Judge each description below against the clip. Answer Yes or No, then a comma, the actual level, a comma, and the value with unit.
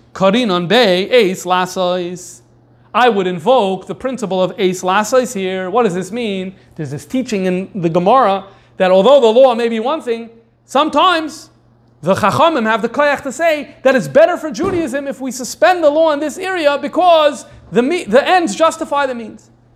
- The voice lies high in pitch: Yes, high, 235 Hz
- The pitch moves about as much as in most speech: No, wide, 7.4 semitones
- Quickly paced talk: No, average, 165 wpm